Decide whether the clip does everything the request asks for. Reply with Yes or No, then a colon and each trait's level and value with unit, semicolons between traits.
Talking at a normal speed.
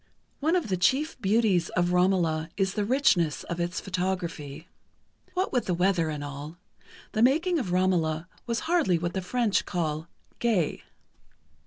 Yes: average, 155 wpm